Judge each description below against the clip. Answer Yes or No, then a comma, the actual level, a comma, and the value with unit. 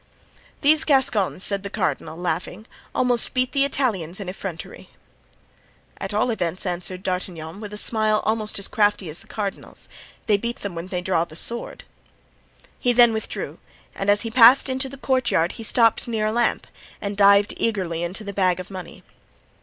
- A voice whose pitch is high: Yes, high, 205 Hz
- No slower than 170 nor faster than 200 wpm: Yes, average, 175 wpm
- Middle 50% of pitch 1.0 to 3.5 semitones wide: No, average, 4.2 semitones